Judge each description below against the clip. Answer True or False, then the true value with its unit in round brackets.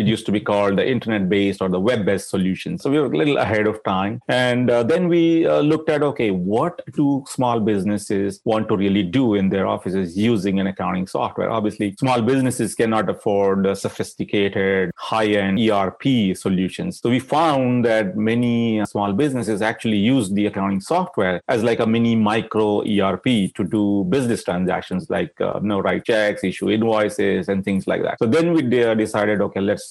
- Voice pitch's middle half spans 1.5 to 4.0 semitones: True (3.3 semitones)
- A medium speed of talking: True (190 wpm)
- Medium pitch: False (105 Hz)